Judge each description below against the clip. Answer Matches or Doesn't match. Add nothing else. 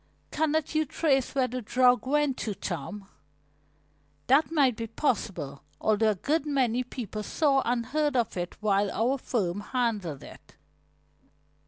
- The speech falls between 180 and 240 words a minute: Doesn't match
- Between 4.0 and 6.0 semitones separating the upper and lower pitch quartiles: Matches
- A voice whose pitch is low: Doesn't match